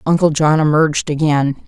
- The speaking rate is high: No, average, 145 wpm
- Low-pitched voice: No, medium, 150 Hz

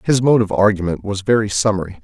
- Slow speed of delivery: No, fast, 205 wpm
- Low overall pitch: Yes, low, 100 Hz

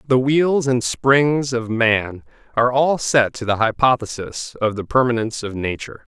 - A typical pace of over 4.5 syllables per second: Yes, 4.7 syllables/s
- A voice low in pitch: Yes, low, 120 Hz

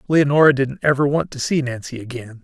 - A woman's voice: No, male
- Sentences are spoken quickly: No, average, 195 wpm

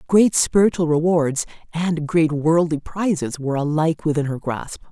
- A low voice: No, medium, 160 Hz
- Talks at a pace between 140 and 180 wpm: Yes, average, 145 wpm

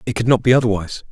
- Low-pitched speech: Yes, low, 115 Hz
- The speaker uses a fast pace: Yes, fast, 270 wpm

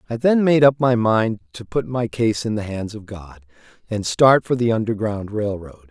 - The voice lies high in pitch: No, low, 110 Hz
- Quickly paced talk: Yes, fast, 225 wpm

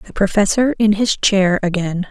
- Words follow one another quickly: No, average, 170 wpm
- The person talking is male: No, female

